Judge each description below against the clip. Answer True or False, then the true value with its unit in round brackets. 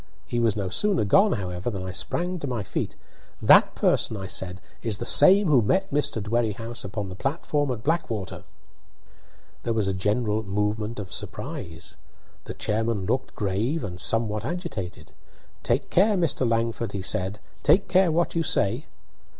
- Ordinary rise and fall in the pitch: False (6.7 semitones)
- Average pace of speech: True (165 wpm)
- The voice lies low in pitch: True (115 Hz)